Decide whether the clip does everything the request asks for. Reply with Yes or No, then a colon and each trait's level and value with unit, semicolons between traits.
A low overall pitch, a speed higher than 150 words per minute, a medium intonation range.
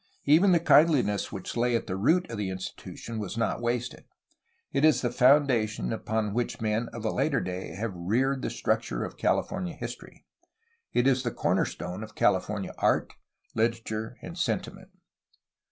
Yes: low, 115 Hz; average, 170 wpm; average, 4.2 semitones